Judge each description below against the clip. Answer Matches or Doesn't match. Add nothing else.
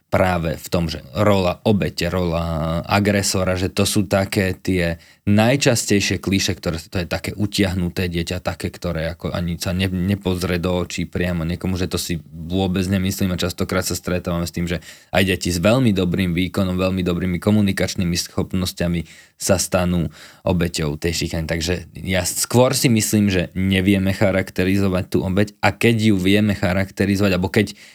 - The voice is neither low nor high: Doesn't match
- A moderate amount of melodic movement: Doesn't match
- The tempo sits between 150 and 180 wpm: Matches